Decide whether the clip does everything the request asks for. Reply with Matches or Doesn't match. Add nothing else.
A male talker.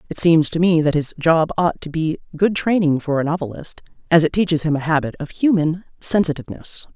Doesn't match